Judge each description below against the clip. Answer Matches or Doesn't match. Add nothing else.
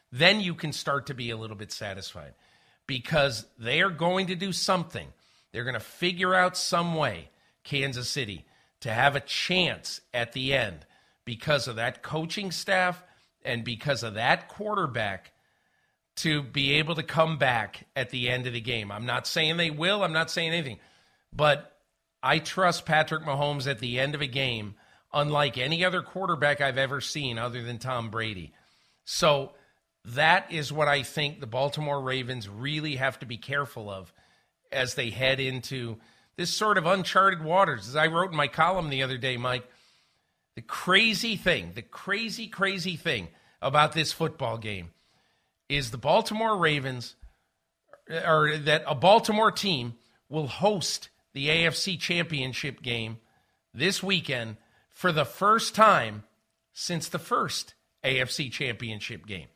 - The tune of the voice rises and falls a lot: Matches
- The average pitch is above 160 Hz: Doesn't match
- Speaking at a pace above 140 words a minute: Matches